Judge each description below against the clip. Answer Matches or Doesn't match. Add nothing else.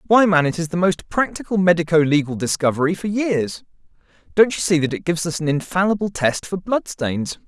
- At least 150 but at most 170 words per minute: Doesn't match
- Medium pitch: Matches